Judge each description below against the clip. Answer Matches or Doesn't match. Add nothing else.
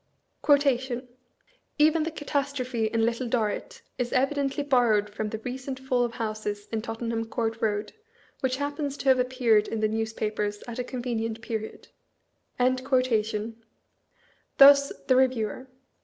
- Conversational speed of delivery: Doesn't match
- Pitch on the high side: Matches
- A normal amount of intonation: Matches